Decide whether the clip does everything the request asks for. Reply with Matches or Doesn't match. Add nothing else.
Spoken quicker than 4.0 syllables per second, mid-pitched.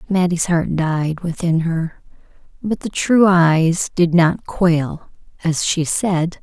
Doesn't match